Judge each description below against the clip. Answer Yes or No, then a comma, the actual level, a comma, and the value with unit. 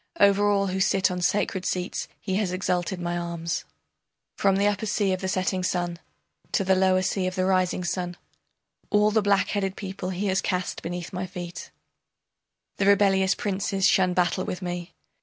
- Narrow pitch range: Yes, narrow, 1.6 semitones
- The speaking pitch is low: No, medium, 185 Hz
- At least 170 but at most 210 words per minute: Yes, average, 175 wpm